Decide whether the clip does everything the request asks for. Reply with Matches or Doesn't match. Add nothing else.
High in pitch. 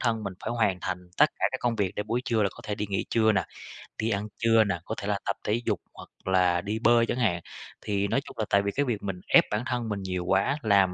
Doesn't match